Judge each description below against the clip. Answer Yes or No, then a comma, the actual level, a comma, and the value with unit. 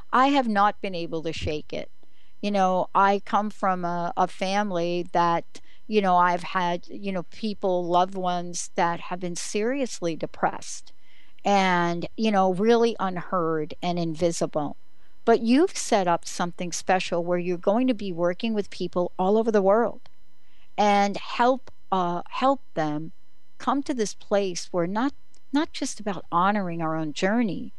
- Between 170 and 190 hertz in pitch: Yes, medium, 185 Hz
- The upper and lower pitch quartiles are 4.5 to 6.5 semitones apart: No, average, 3.4 semitones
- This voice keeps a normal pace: Yes, average, 160 wpm